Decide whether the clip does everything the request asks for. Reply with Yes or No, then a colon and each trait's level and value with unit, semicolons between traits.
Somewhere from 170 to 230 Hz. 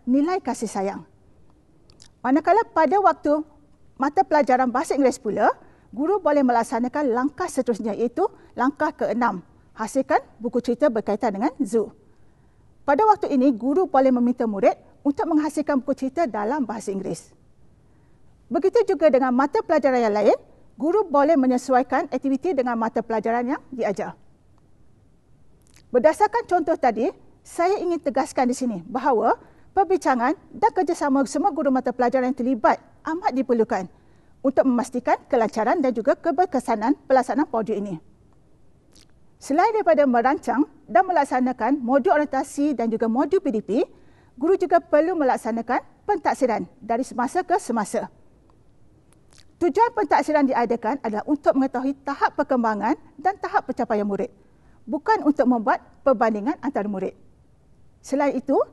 No: very high, 275 Hz